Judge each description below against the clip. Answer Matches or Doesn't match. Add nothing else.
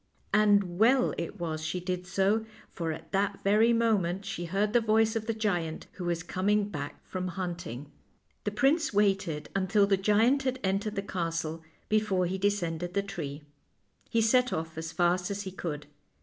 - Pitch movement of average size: Matches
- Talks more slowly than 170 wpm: Doesn't match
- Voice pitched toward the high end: Matches